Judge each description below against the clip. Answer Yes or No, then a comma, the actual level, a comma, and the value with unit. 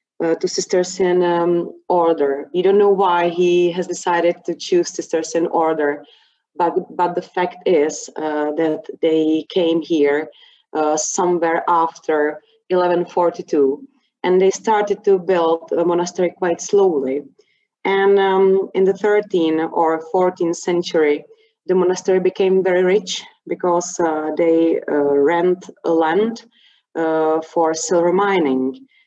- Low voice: No, medium, 175 Hz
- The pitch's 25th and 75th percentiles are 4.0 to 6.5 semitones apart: No, average, 2.8 semitones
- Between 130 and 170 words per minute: Yes, slow, 135 wpm